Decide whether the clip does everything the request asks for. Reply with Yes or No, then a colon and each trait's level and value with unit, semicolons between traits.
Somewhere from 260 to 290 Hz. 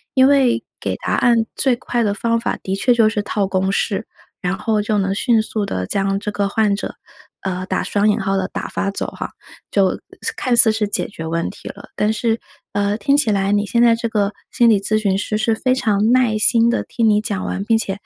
No: high, 215 Hz